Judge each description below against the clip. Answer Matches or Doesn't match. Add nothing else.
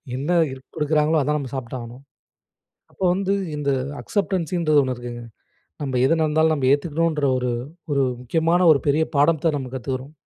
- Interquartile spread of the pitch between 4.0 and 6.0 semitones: Doesn't match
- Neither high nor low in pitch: Matches